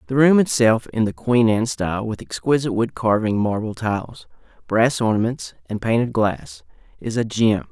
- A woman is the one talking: No, male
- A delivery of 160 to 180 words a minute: Yes, average, 170 wpm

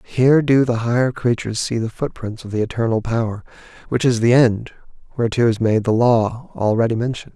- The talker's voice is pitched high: No, low, 115 Hz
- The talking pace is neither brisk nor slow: Yes, average, 190 wpm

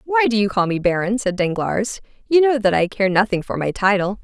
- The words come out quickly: Yes, fast, 240 wpm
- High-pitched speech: Yes, high, 205 Hz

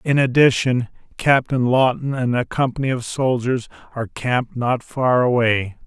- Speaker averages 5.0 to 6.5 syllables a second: No, 4.7 syllables/s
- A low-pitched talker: Yes, low, 125 Hz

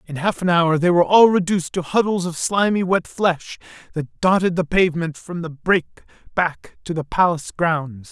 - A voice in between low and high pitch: Yes, medium, 175 Hz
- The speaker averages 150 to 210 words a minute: Yes, average, 190 wpm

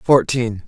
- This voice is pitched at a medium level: No, low, 120 Hz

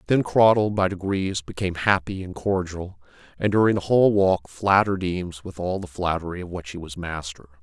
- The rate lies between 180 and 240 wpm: Yes, average, 190 wpm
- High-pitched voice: No, very low, 90 Hz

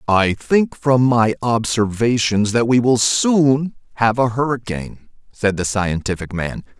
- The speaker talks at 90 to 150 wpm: Yes, average, 140 wpm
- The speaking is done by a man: Yes, male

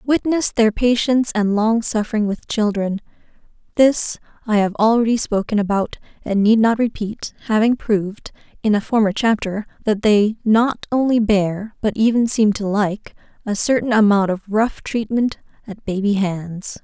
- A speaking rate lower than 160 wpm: Yes, average, 145 wpm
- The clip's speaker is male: No, female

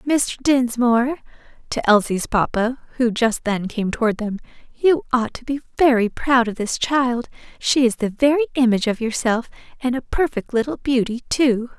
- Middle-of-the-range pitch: No, high, 245 Hz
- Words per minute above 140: Yes, average, 160 wpm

